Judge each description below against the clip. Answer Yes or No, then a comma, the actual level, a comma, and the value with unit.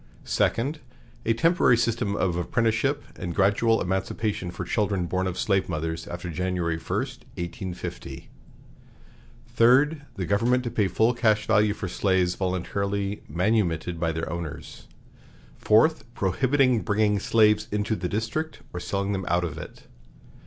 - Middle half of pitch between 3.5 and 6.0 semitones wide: Yes, average, 4.2 semitones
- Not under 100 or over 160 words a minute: Yes, average, 140 wpm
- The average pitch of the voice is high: No, low, 100 Hz